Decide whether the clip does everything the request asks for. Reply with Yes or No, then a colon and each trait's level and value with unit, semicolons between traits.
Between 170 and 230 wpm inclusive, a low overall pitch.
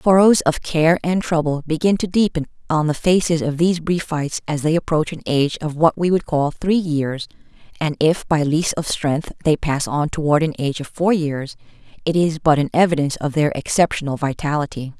No: average, 200 wpm; medium, 155 Hz